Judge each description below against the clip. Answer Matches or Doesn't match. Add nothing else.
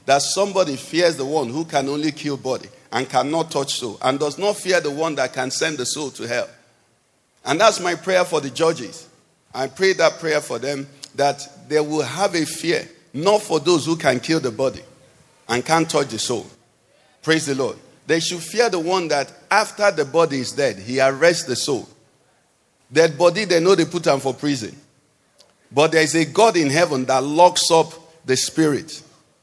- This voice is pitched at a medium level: Matches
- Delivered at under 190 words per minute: Doesn't match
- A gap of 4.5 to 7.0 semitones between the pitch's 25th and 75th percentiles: Doesn't match